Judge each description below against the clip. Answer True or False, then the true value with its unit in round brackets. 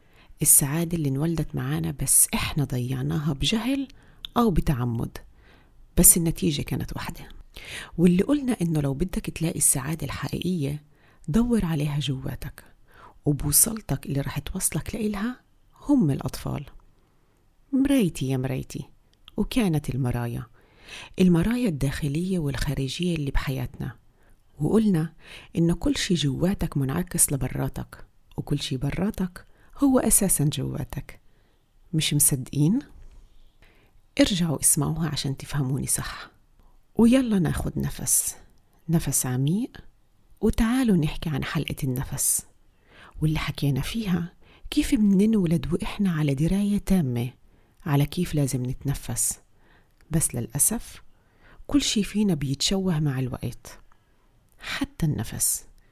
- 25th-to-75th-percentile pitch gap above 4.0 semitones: True (5.5 semitones)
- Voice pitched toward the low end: False (150 Hz)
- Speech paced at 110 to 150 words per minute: False (100 wpm)